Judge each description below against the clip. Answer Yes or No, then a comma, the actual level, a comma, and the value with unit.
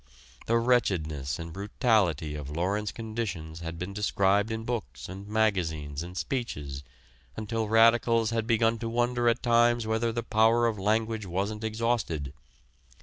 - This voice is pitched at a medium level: No, low, 110 Hz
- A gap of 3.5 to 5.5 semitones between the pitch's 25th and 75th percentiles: Yes, average, 5.2 semitones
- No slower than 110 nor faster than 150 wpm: Yes, average, 145 wpm